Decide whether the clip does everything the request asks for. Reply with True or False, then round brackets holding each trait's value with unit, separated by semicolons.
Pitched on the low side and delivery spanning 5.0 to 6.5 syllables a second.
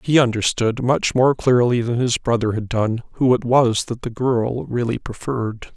False (120 Hz; 4.6 syllables/s)